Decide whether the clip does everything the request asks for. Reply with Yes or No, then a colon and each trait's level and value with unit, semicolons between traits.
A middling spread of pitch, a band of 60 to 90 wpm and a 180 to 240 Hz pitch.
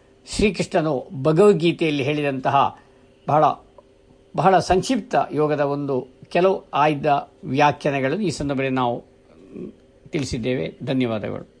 No: average, 4.5 semitones; average, 85 wpm; medium, 145 Hz